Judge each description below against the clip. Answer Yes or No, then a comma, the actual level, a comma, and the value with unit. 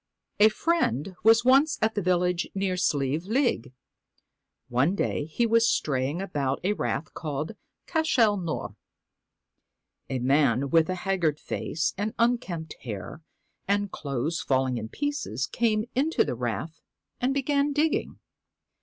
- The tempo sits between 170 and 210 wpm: No, slow, 135 wpm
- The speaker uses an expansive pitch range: Yes, wide, 8.5 semitones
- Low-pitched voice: No, medium, 180 Hz